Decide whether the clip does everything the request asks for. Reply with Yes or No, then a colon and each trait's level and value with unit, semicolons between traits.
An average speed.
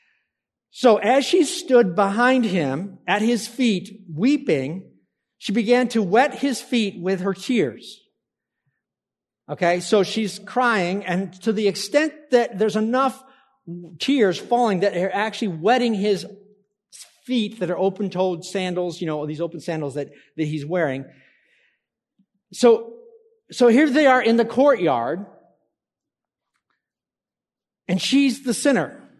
No: slow, 130 wpm